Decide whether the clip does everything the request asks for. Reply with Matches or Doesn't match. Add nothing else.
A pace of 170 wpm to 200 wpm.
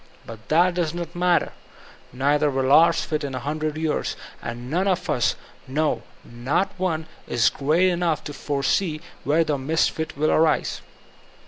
Doesn't match